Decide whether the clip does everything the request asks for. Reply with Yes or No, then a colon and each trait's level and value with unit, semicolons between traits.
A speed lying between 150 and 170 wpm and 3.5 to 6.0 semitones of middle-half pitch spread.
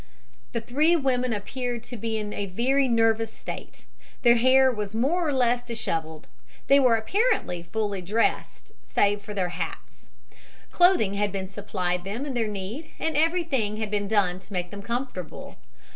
Yes: average, 165 wpm; average, 4.4 semitones